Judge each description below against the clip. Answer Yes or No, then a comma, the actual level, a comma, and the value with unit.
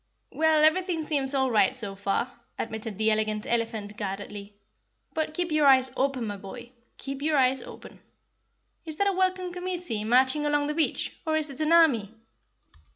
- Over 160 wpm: Yes, average, 170 wpm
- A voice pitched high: Yes, very high, 270 Hz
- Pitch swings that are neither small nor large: No, wide, 6.1 semitones